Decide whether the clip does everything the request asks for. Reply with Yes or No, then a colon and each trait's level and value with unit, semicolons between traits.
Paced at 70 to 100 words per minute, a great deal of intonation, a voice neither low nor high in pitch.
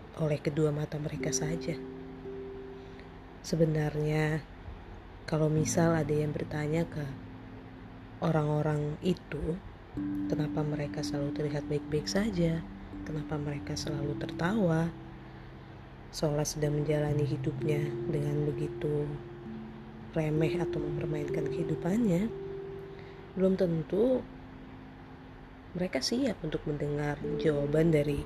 No: average, 90 wpm; average, 3.5 semitones; medium, 150 Hz